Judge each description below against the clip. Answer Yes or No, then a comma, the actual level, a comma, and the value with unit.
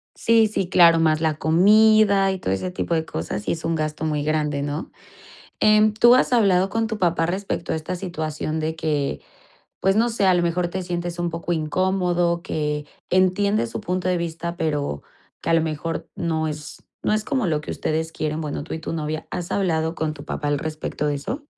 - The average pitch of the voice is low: No, medium, 165 Hz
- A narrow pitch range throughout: No, average, 3.3 semitones